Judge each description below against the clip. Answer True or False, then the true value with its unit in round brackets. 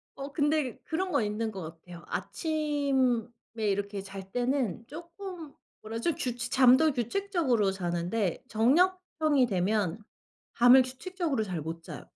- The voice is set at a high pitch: True (245 Hz)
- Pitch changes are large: True (7.0 semitones)